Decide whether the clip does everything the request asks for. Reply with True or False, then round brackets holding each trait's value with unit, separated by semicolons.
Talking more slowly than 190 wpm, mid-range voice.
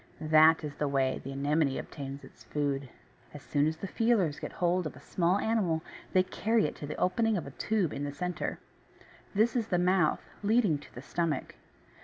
False (200 wpm; 160 Hz)